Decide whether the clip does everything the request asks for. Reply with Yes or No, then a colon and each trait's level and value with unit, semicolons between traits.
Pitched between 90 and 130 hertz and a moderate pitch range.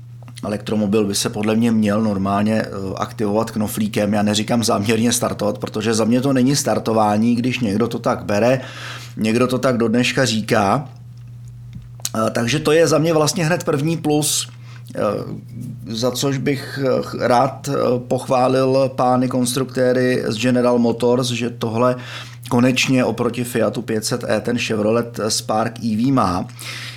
No: low, 120 Hz; narrow, 2.2 semitones